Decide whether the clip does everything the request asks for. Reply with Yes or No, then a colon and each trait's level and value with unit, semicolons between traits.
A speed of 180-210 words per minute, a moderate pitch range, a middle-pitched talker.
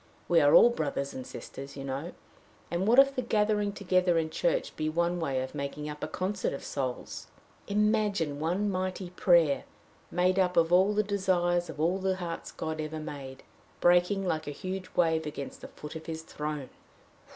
Yes: average, 185 wpm; average, 4.0 semitones; medium, 175 Hz